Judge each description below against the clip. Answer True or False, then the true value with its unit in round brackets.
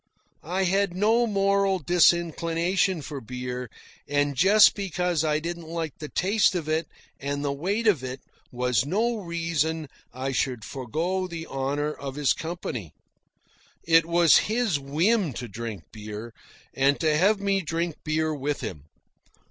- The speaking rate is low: False (150 wpm)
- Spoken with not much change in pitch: False (5.0 semitones)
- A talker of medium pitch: True (160 Hz)